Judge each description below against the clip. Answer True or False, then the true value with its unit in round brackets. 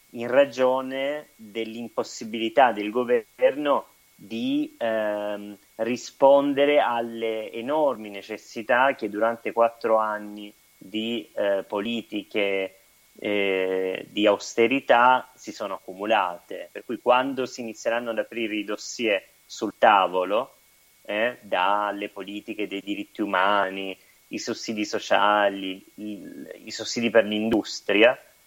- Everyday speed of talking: False (105 wpm)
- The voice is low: True (110 Hz)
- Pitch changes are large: False (2.6 semitones)